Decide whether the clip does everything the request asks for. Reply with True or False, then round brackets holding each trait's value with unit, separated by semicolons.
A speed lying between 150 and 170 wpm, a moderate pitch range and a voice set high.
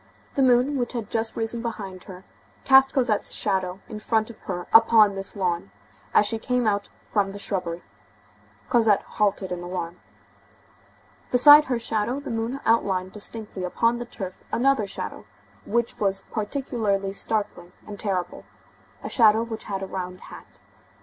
True (155 wpm; 3.4 semitones; 210 Hz)